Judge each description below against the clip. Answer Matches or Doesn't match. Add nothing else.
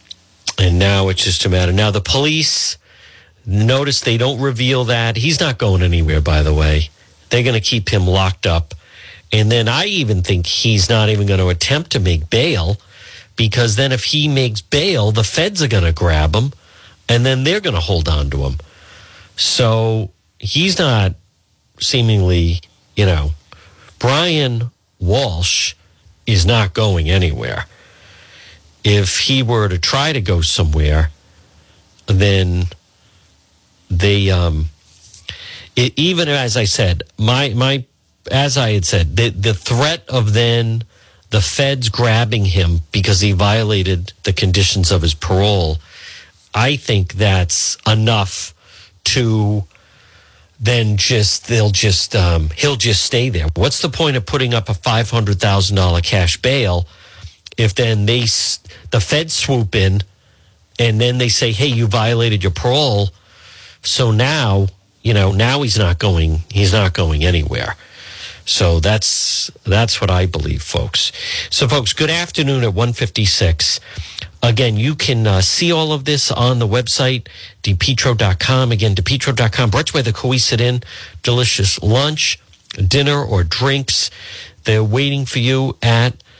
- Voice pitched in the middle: Doesn't match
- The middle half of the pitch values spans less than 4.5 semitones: Doesn't match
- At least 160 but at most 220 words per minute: Doesn't match